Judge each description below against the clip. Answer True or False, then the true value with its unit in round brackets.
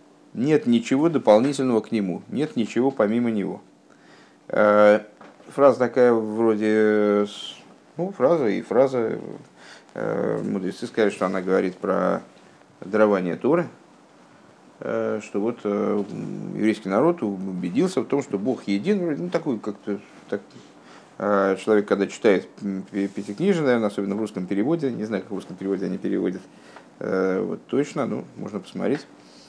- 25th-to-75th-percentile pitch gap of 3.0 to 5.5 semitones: False (2.4 semitones)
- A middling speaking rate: True (120 wpm)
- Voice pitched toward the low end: True (105 Hz)